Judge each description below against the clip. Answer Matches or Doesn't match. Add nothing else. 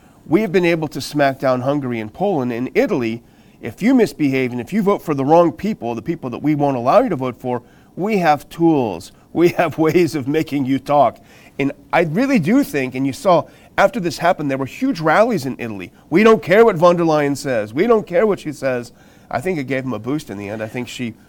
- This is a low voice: Doesn't match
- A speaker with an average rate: Doesn't match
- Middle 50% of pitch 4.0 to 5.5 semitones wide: Matches